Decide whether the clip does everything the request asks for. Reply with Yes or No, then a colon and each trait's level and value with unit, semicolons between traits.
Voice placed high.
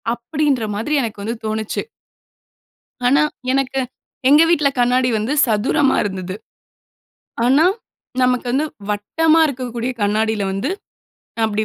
Yes: high, 245 Hz